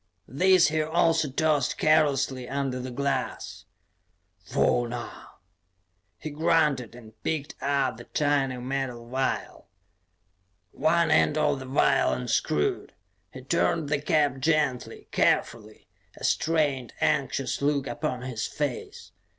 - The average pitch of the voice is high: No, medium, 140 Hz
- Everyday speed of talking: No, slow, 115 wpm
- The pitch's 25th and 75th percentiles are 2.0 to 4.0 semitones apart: Yes, average, 3.5 semitones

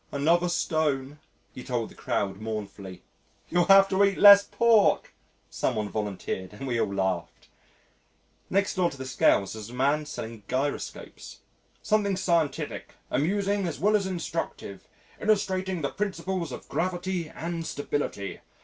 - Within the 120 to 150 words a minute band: Yes, average, 140 wpm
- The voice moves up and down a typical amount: No, wide, 8.5 semitones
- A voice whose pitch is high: No, medium, 155 Hz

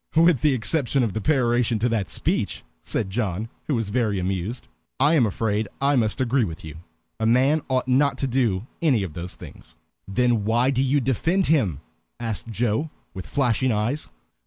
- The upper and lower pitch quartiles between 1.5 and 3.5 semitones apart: No, average, 4.2 semitones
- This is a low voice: Yes, low, 120 Hz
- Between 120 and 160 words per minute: No, average, 190 wpm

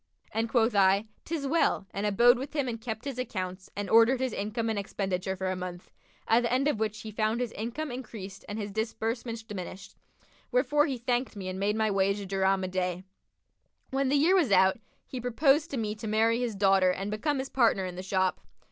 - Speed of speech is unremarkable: No, fast, 220 wpm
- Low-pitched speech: No, high, 220 Hz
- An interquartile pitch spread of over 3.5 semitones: Yes, average, 4.2 semitones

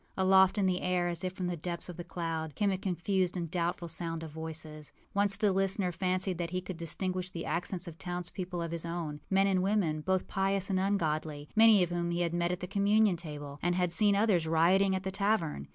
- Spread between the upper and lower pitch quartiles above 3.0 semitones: No, narrow, 2.4 semitones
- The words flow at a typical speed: No, fast, 230 wpm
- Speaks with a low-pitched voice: No, medium, 180 Hz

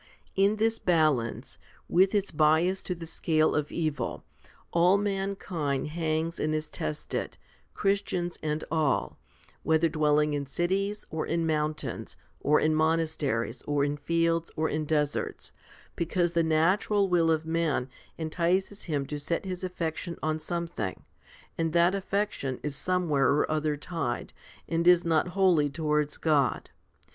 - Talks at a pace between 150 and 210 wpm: No, average, 140 wpm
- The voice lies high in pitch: No, medium, 160 Hz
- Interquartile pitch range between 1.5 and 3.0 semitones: Yes, average, 2.7 semitones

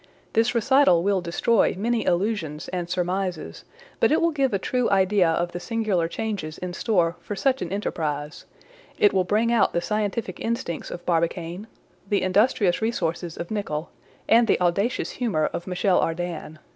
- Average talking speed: Yes, average, 165 wpm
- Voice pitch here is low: No, medium, 185 Hz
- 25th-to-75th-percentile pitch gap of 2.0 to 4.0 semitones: No, average, 4.4 semitones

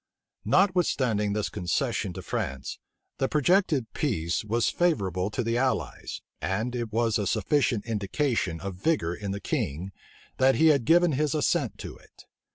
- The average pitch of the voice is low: Yes, low, 115 Hz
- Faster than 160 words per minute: No, average, 155 wpm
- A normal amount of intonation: No, wide, 7.0 semitones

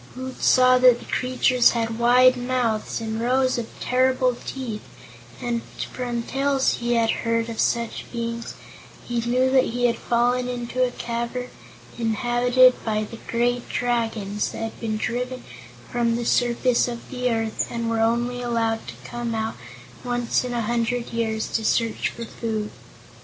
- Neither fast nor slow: Yes, average, 160 wpm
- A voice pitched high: Yes, high, 240 Hz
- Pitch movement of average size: No, narrow, 1.4 semitones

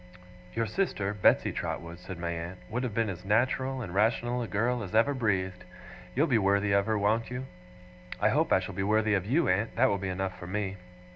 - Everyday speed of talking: No, fast, 220 wpm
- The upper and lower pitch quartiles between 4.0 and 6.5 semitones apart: No, average, 3.5 semitones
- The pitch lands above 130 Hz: No, low, 105 Hz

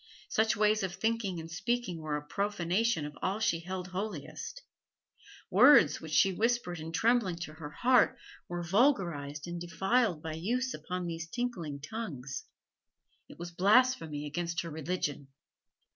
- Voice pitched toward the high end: No, medium, 180 Hz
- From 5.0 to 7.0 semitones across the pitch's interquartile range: Yes, wide, 5.4 semitones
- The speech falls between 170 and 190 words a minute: No, average, 145 wpm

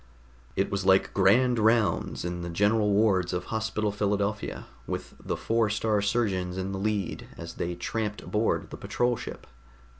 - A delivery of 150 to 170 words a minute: Yes, average, 160 wpm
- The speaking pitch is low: Yes, low, 105 Hz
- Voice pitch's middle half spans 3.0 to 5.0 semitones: No, narrow, 2.6 semitones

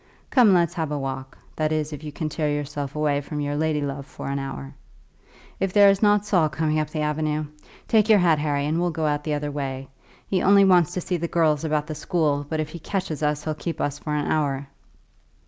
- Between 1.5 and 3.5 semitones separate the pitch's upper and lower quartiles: Yes, narrow, 2.6 semitones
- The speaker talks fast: Yes, fast, 235 wpm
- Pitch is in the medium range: Yes, medium, 155 Hz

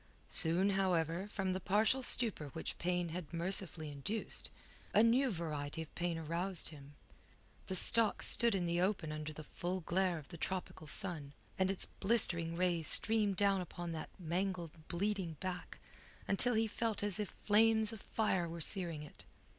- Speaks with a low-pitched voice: No, medium, 180 Hz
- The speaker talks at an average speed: Yes, average, 165 wpm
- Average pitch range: Yes, average, 3.6 semitones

